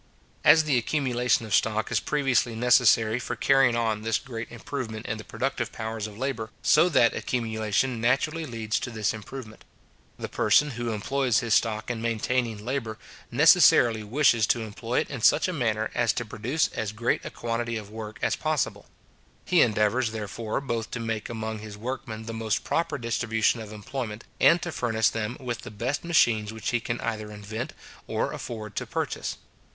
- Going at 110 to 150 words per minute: No, average, 180 wpm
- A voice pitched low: Yes, low, 115 Hz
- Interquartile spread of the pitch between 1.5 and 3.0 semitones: Yes, narrow, 2.4 semitones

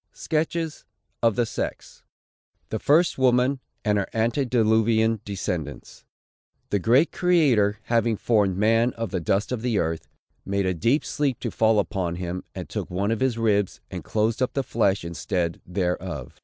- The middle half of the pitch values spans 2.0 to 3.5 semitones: No, average, 4.2 semitones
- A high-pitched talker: No, low, 110 Hz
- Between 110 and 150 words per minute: No, average, 160 wpm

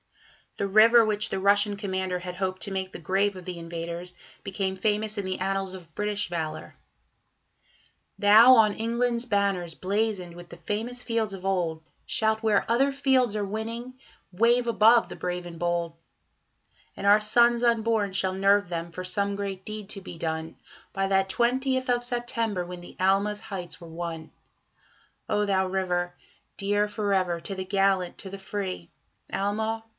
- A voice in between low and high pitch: No, high, 195 Hz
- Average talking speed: Yes, average, 170 wpm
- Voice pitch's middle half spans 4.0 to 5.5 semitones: No, average, 3.2 semitones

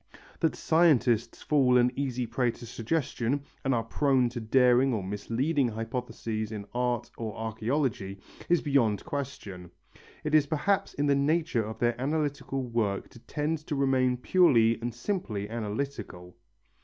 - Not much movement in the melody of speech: No, average, 4.0 semitones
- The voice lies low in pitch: Yes, low, 125 Hz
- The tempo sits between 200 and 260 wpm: No, average, 145 wpm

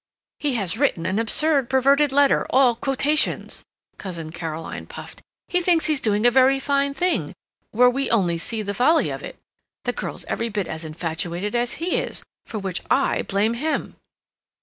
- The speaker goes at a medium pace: Yes, average, 170 wpm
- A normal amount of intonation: No, wide, 6.3 semitones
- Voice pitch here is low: No, high, 240 Hz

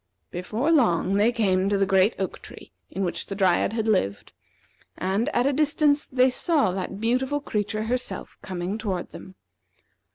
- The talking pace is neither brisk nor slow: Yes, average, 165 wpm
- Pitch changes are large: No, average, 4.9 semitones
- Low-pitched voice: No, high, 210 Hz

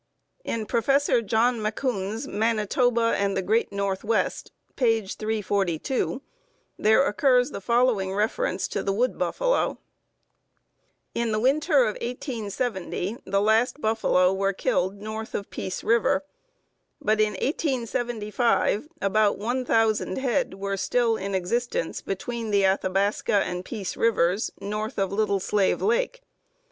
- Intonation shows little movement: No, average, 3.4 semitones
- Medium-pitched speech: No, high, 215 Hz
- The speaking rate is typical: No, slow, 125 wpm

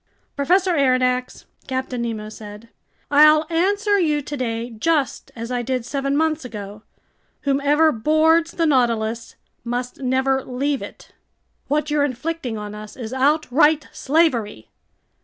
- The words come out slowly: Yes, slow, 125 wpm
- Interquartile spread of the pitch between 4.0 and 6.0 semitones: Yes, average, 4.5 semitones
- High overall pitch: Yes, very high, 265 Hz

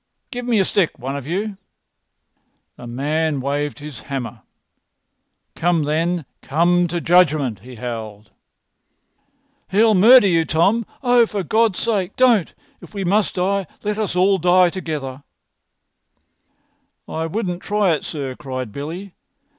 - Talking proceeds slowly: Yes, slow, 130 wpm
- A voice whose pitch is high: No, medium, 175 Hz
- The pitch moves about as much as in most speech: No, wide, 5.9 semitones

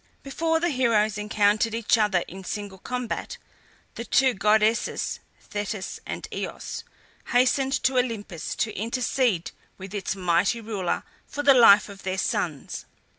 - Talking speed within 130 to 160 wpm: Yes, slow, 135 wpm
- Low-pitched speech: No, high, 215 Hz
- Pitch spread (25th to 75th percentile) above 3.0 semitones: Yes, average, 4.1 semitones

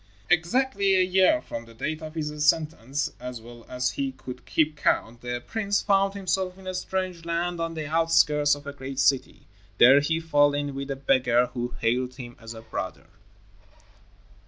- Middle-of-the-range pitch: Yes, medium, 145 Hz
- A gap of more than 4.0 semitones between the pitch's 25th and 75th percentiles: Yes, average, 5.3 semitones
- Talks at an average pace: Yes, average, 180 wpm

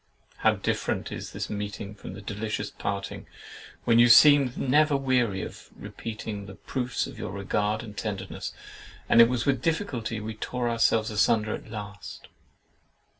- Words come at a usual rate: Yes, average, 155 wpm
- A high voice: No, low, 110 Hz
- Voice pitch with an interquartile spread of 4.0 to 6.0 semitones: No, average, 3.3 semitones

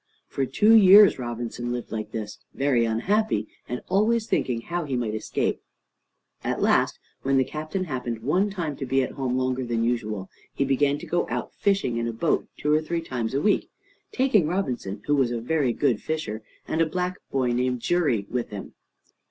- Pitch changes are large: Yes, wide, 6.0 semitones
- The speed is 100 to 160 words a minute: No, average, 195 wpm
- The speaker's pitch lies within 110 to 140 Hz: Yes, low, 135 Hz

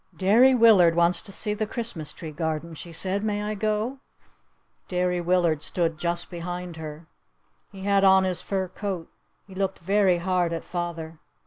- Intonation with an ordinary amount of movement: Yes, average, 3.0 semitones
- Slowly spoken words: No, average, 165 wpm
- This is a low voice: No, medium, 180 Hz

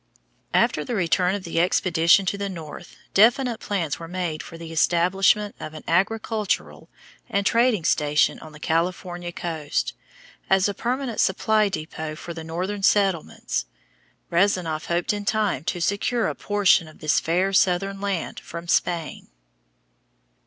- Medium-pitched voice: Yes, medium, 180 Hz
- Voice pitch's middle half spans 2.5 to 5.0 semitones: Yes, average, 3.5 semitones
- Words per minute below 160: Yes, average, 145 wpm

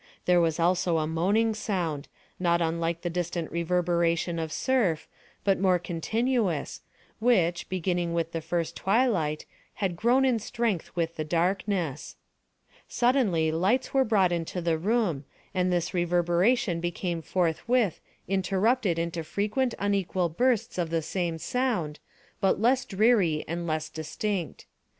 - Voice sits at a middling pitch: Yes, medium, 175 Hz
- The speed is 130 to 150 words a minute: Yes, slow, 135 wpm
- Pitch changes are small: No, average, 4.0 semitones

